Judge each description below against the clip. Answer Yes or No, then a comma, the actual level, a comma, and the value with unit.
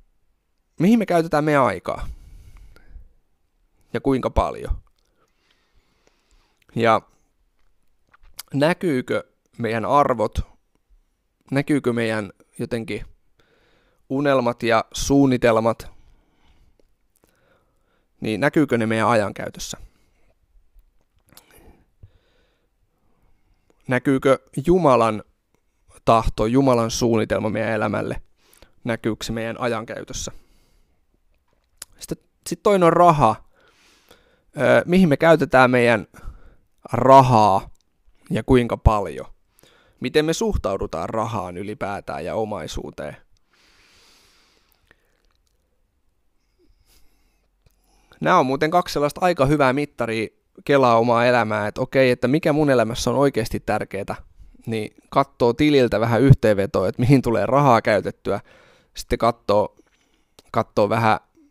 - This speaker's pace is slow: Yes, slow, 85 wpm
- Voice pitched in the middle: No, low, 120 Hz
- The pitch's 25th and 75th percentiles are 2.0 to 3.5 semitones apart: No, average, 4.6 semitones